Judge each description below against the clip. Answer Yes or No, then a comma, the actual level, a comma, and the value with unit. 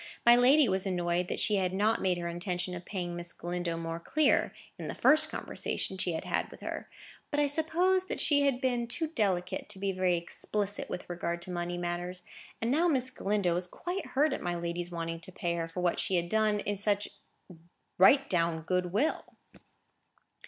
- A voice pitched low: No, medium, 185 Hz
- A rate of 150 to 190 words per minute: No, average, 200 wpm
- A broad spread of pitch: Yes, wide, 5.7 semitones